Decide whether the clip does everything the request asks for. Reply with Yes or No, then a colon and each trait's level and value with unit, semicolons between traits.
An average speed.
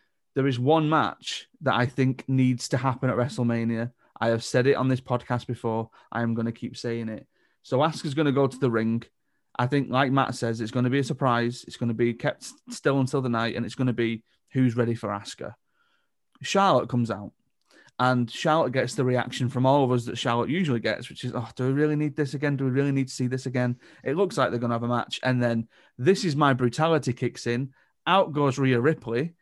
No: fast, 245 wpm